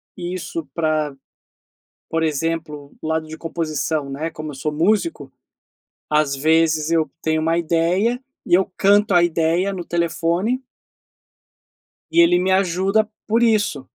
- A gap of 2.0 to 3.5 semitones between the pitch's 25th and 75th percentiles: Yes, average, 2.9 semitones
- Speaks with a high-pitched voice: No, medium, 165 Hz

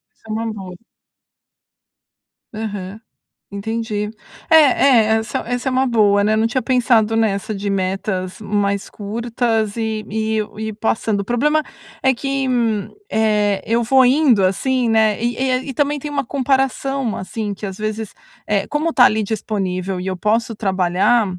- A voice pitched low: No, high, 220 Hz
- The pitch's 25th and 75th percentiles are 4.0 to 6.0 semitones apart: No, average, 3.5 semitones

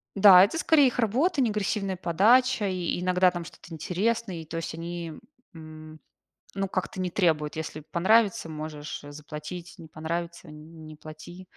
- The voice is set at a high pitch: No, medium, 175 Hz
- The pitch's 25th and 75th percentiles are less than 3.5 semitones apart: No, average, 3.9 semitones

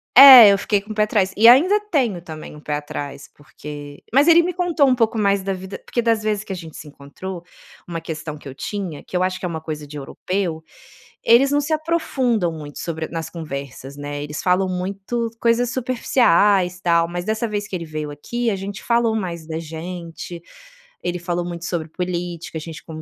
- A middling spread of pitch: No, wide, 5.7 semitones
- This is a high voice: No, medium, 180 Hz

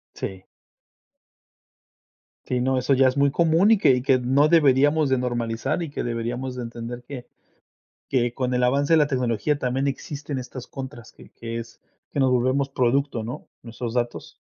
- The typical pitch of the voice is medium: No, low, 130 Hz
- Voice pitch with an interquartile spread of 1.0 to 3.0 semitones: Yes, narrow, 2.6 semitones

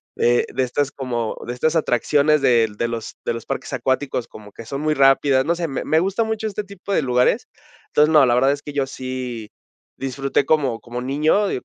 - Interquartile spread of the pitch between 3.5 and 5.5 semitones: Yes, average, 3.8 semitones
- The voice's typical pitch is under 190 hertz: Yes, low, 135 Hz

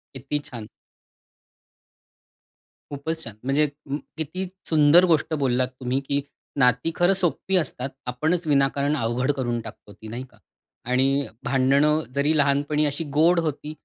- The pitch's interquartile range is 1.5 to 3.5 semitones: Yes, average, 3.2 semitones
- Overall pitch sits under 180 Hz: Yes, medium, 140 Hz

